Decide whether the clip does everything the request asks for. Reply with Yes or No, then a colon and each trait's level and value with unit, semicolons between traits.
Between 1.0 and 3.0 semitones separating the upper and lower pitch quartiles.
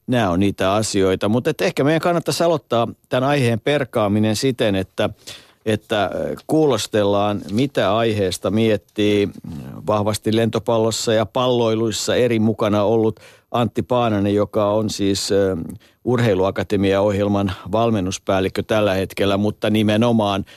Yes: narrow, 2.5 semitones